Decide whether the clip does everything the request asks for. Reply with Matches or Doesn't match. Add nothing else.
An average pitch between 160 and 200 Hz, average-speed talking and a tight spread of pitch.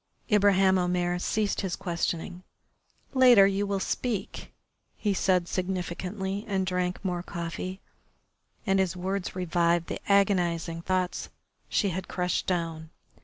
Doesn't match